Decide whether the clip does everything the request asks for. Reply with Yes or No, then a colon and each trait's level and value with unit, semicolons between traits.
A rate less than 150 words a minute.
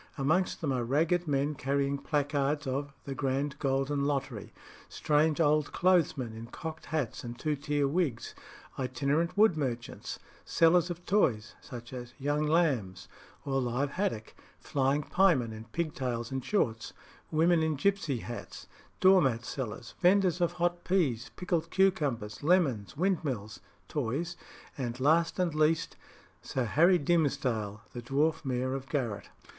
Yes: average, 140 wpm